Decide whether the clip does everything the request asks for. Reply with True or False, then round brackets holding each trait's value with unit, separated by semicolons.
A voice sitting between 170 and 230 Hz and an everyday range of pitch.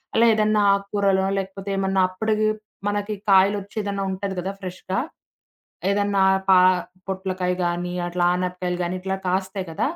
False (190 Hz; 1.5 semitones)